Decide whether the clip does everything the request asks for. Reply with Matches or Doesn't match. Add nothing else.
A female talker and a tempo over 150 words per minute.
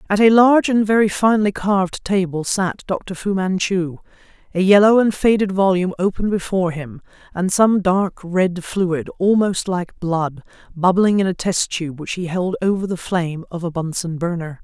Matches